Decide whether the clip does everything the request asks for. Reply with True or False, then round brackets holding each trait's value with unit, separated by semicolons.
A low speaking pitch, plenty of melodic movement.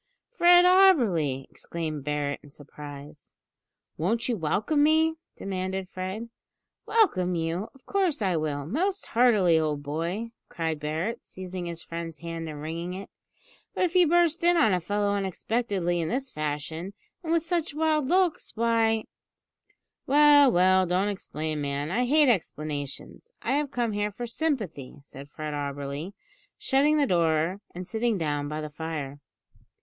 False (185 Hz; 8.9 semitones)